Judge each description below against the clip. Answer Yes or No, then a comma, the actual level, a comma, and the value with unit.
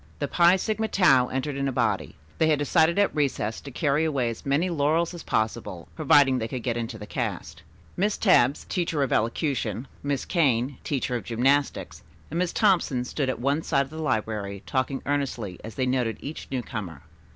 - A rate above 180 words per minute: Yes, average, 190 wpm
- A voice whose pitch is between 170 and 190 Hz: No, medium, 140 Hz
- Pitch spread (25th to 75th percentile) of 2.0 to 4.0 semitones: No, average, 4.7 semitones